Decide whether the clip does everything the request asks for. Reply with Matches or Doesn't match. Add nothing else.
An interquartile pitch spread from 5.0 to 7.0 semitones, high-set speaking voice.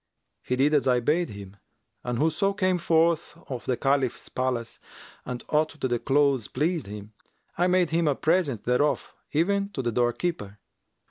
Doesn't match